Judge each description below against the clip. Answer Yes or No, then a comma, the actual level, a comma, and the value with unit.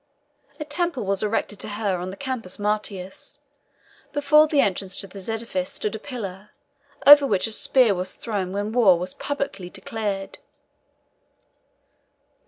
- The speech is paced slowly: No, average, 145 wpm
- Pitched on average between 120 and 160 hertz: No, high, 210 Hz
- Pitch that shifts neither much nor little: No, wide, 5.8 semitones